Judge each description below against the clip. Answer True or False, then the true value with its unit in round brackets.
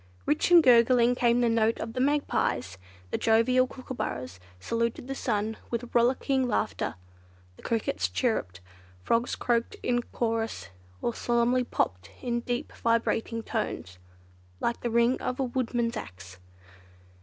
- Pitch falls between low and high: False (235 Hz)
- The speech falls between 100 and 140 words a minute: True (135 wpm)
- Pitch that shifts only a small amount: True (1.9 semitones)